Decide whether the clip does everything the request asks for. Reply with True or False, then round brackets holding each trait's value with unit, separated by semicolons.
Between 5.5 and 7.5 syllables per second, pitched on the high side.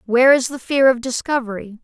True (6.0 syllables/s; 250 Hz)